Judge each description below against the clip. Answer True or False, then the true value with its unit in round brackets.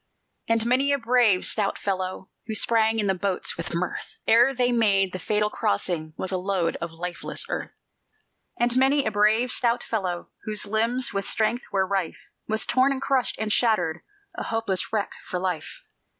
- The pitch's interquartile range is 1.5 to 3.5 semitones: False (4.1 semitones)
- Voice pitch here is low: False (215 Hz)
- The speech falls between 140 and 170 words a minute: False (180 wpm)